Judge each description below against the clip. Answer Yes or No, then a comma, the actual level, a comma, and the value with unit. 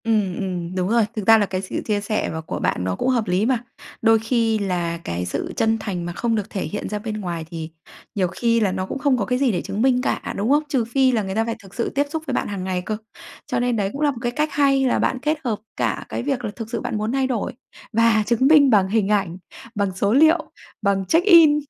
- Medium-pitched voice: No, high, 220 Hz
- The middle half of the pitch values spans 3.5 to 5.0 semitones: Yes, average, 4.6 semitones